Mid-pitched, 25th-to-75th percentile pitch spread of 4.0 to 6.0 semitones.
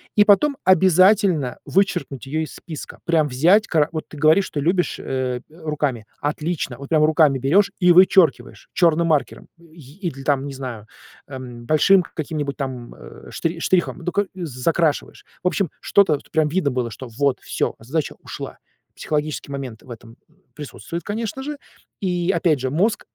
Yes: medium, 155 Hz; average, 4.6 semitones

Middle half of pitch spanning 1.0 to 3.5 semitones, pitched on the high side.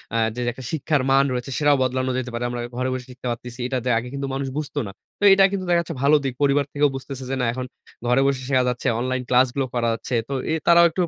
No: narrow, 2.4 semitones; low, 130 Hz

